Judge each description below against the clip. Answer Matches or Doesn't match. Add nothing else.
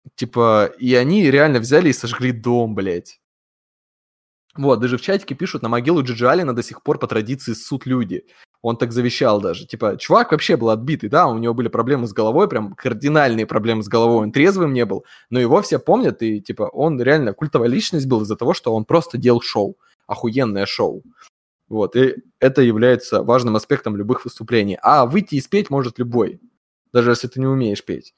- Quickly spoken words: Matches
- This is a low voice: Matches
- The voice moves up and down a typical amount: Matches